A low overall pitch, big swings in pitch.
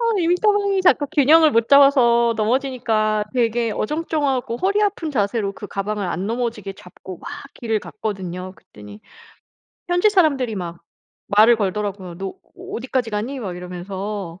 No: high, 230 Hz; wide, 5.9 semitones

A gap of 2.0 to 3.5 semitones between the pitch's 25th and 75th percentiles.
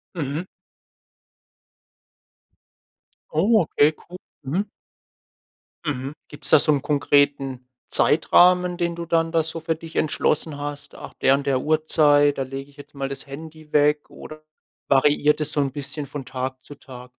Yes: narrow, 2.5 semitones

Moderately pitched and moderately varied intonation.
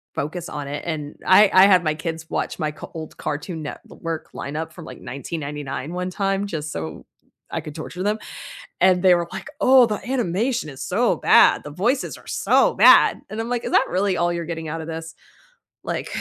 Yes: medium, 170 Hz; average, 4.0 semitones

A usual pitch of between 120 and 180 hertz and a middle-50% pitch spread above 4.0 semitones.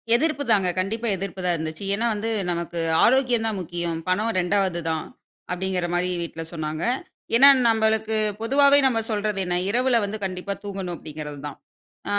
No: high, 195 Hz; average, 4.6 semitones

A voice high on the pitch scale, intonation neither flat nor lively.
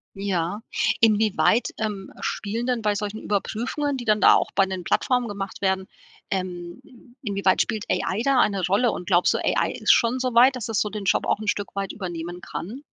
Yes: high, 205 Hz; average, 3.3 semitones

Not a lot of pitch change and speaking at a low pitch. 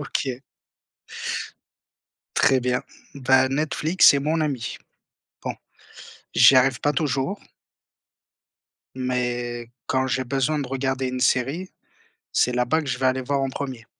Yes: narrow, 2.1 semitones; low, 130 Hz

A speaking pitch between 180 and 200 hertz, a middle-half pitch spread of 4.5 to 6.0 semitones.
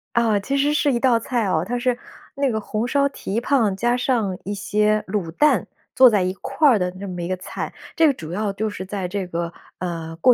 No: high, 215 Hz; average, 5.1 semitones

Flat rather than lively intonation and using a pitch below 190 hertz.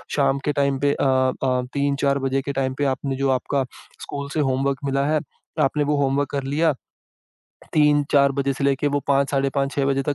Yes: narrow, 0.9 semitones; medium, 140 Hz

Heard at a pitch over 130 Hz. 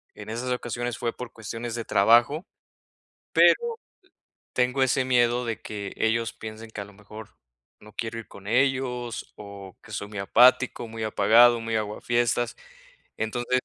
No: low, 115 Hz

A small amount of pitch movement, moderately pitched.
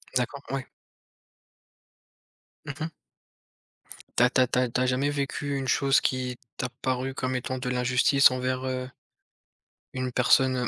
No: narrow, 1.0 semitones; low, 130 Hz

